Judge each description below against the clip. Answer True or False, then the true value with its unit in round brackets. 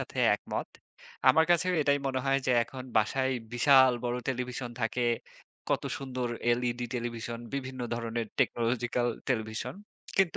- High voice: False (125 Hz)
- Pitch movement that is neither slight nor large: False (2.0 semitones)